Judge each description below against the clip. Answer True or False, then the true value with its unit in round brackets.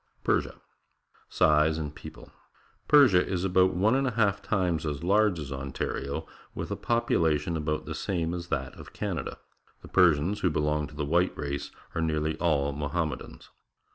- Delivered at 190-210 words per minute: False (170 wpm)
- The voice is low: True (80 Hz)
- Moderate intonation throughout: True (3.8 semitones)